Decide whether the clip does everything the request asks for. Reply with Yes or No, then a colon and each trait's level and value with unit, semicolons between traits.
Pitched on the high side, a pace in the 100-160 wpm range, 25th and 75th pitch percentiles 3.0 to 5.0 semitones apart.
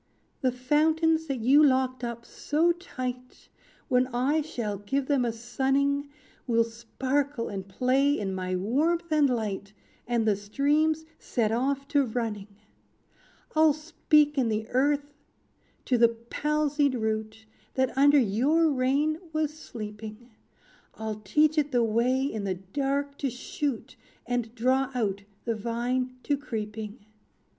Yes: very high, 255 Hz; slow, 135 wpm; average, 4.3 semitones